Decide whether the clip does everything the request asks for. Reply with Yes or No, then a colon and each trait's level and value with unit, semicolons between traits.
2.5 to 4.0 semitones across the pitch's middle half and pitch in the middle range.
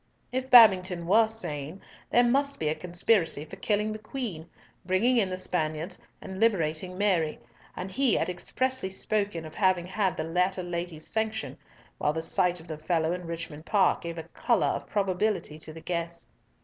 No: average, 4.4 semitones; medium, 180 Hz